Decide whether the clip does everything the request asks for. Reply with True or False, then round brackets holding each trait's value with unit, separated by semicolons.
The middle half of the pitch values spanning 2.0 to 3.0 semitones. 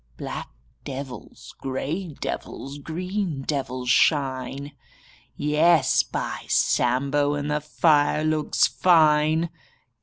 True (2.4 semitones)